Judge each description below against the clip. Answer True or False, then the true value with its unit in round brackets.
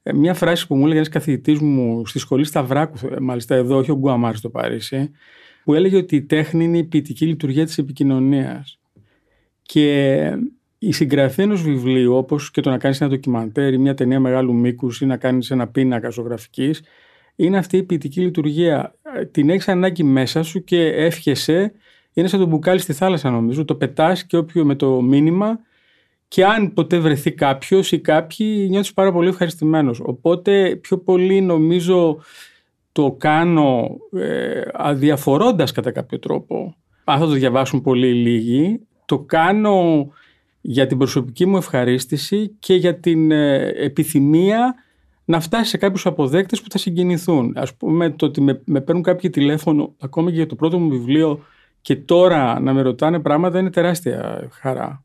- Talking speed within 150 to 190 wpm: True (165 wpm)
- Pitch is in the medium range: True (155 Hz)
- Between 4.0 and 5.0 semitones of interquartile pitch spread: True (4.5 semitones)